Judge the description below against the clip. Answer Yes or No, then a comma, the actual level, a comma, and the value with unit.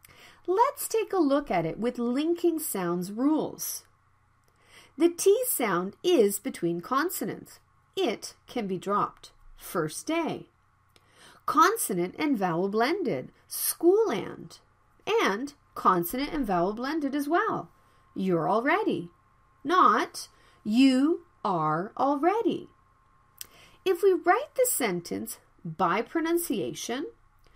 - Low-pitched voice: No, very high, 285 Hz